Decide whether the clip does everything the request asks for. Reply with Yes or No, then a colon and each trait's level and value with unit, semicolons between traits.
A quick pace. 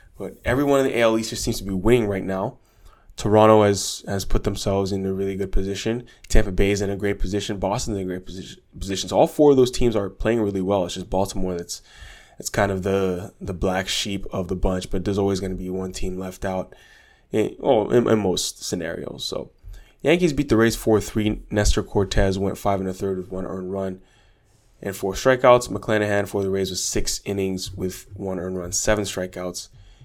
Yes: fast, 220 wpm